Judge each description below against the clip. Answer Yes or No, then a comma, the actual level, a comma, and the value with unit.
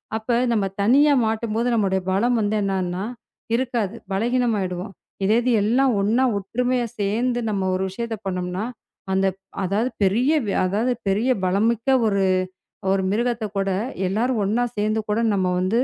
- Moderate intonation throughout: Yes, average, 3.6 semitones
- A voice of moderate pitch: No, high, 215 Hz